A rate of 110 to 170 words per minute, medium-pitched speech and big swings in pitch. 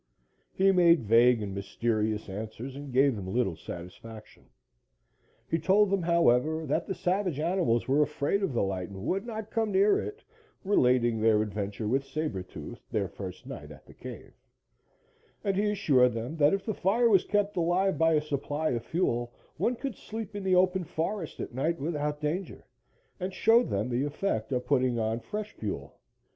No: average, 180 wpm; medium, 150 Hz; wide, 8.4 semitones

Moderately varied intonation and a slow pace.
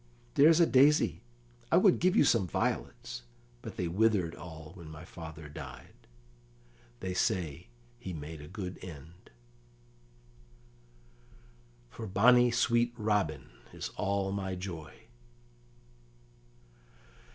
No: wide, 5.8 semitones; slow, 110 wpm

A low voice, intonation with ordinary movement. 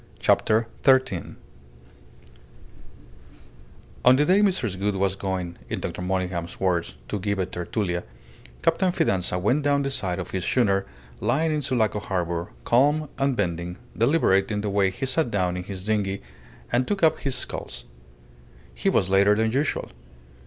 No: low, 105 Hz; wide, 6.0 semitones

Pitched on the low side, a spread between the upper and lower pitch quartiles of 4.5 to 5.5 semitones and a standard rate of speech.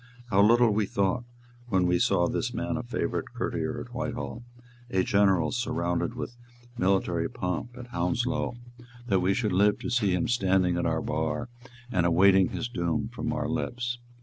Yes: low, 100 Hz; average, 5.0 semitones; average, 170 wpm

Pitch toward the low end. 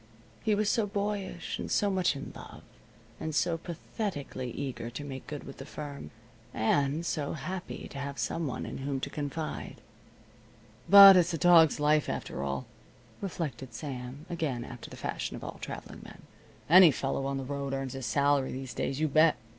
No: medium, 145 Hz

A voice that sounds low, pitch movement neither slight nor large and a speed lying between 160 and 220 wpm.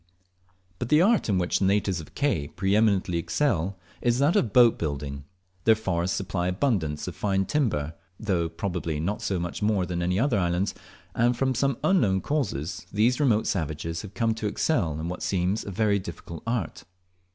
Yes: very low, 95 Hz; average, 5.0 semitones; average, 180 wpm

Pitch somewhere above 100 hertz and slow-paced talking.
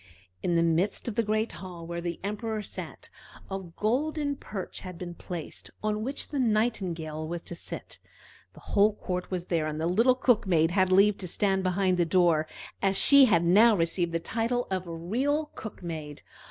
No: high, 190 Hz; average, 195 wpm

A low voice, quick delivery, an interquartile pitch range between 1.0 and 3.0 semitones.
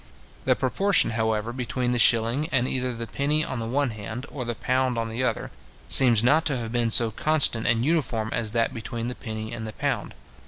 Yes: low, 120 Hz; fast, 210 wpm; narrow, 2.6 semitones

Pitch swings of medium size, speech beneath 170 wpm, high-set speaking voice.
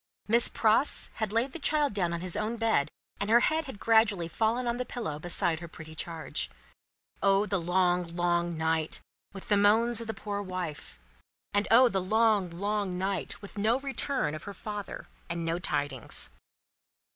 No: average, 4.8 semitones; average, 180 wpm; high, 200 Hz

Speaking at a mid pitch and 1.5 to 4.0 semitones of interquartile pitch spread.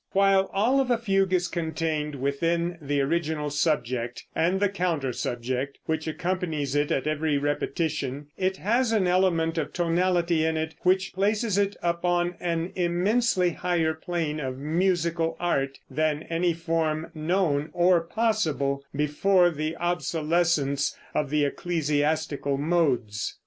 Yes: medium, 165 Hz; average, 3.3 semitones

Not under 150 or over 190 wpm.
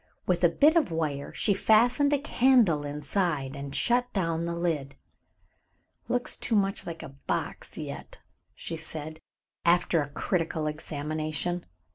No: average, 140 wpm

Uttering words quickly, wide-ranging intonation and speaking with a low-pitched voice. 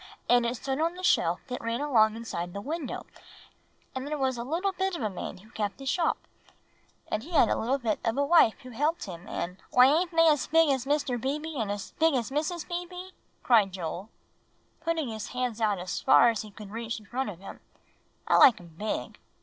No: fast, 215 wpm; wide, 6.1 semitones; very high, 250 Hz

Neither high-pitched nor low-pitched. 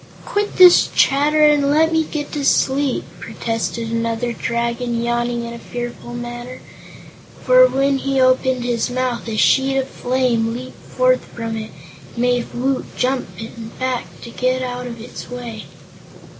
No: very high, 250 Hz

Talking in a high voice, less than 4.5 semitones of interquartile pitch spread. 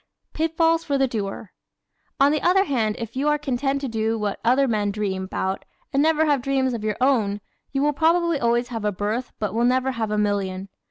No: high, 245 Hz; average, 4.9 semitones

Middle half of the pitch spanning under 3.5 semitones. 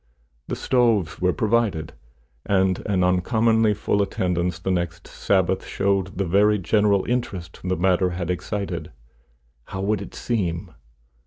Yes: average, 2.7 semitones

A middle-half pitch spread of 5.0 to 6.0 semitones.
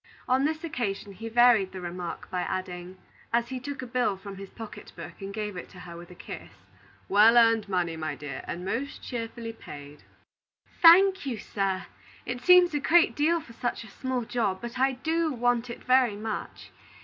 Yes: average, 5.3 semitones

